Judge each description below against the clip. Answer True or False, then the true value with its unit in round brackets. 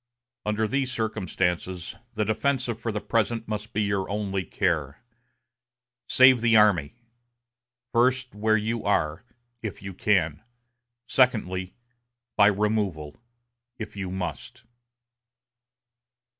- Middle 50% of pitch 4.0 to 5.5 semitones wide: False (3.5 semitones)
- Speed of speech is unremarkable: False (105 wpm)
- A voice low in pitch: True (105 Hz)